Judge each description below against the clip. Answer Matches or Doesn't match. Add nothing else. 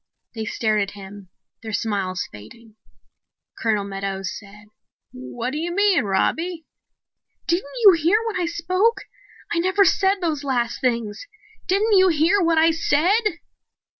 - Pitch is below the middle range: Doesn't match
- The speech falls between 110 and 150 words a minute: Matches